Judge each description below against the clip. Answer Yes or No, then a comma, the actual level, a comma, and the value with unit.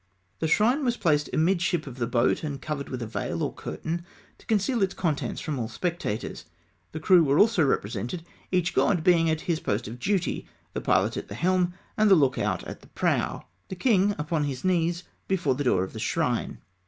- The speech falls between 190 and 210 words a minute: Yes, fast, 205 wpm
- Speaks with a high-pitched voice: No, medium, 165 Hz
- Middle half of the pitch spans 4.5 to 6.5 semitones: Yes, average, 4.9 semitones